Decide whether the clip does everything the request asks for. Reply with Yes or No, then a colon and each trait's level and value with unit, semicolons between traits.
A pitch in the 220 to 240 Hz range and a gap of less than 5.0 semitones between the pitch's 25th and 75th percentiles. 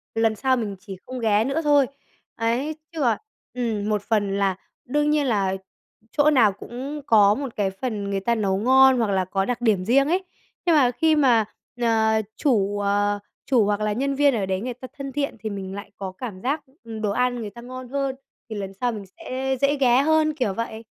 Yes: high, 230 Hz; average, 4.6 semitones